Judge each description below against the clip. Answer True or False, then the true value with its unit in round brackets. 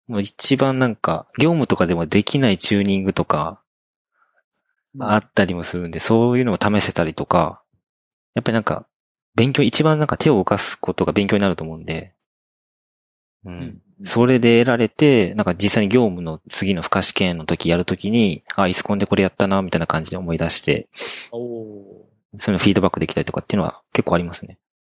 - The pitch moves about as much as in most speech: True (5.0 semitones)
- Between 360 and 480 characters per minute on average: True (385 characters per minute)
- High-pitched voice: False (100 Hz)